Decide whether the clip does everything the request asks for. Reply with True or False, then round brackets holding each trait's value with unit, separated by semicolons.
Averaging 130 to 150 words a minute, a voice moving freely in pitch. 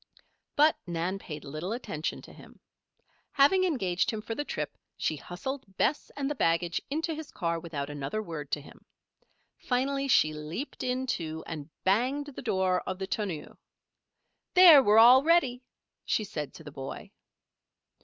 False (160 wpm; 8.8 semitones)